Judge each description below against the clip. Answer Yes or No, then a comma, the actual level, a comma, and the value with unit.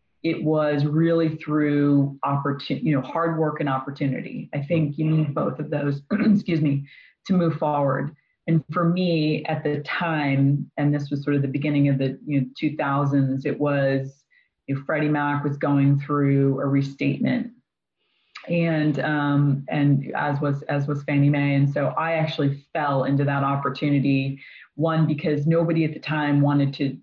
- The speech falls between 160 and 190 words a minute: Yes, average, 170 wpm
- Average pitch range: No, narrow, 1.7 semitones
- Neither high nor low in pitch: Yes, medium, 145 Hz